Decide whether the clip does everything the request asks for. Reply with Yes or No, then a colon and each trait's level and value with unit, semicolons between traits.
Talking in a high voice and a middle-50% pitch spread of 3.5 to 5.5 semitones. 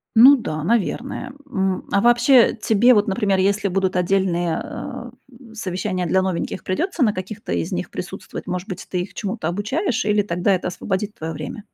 Yes: high, 200 Hz; average, 3.8 semitones